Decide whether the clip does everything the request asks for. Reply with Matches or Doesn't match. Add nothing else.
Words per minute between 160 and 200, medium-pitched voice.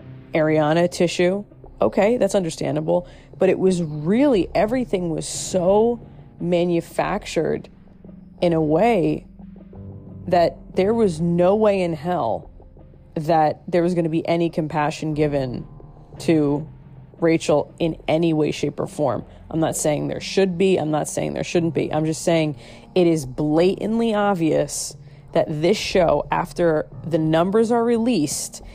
Doesn't match